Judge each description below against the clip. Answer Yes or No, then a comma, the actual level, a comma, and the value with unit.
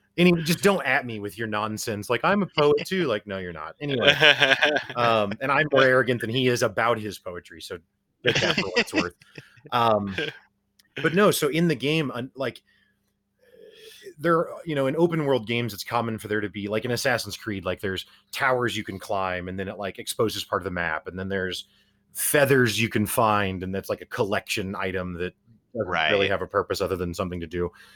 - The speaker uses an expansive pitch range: Yes, wide, 6.3 semitones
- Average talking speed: No, fast, 215 wpm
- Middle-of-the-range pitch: No, low, 115 Hz